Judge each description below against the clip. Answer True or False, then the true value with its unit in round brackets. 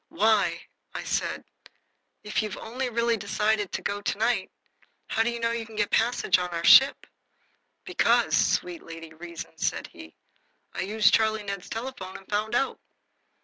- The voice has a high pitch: True (215 Hz)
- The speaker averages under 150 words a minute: False (170 wpm)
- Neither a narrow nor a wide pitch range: True (3.4 semitones)